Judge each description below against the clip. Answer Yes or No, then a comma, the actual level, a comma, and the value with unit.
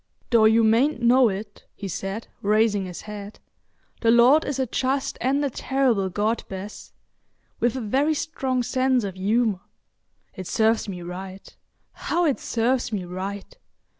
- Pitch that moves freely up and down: No, average, 4.5 semitones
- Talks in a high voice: Yes, high, 225 Hz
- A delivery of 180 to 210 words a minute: No, average, 150 wpm